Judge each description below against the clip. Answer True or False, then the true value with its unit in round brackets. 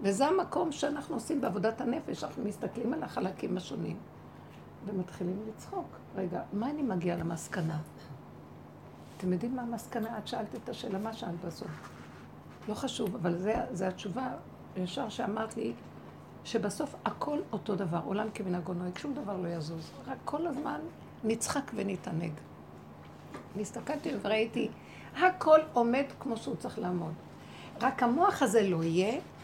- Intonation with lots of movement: True (5.7 semitones)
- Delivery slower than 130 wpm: False (135 wpm)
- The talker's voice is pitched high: True (215 Hz)